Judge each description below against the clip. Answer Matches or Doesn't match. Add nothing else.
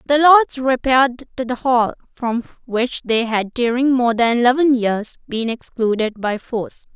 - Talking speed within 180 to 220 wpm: Doesn't match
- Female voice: Matches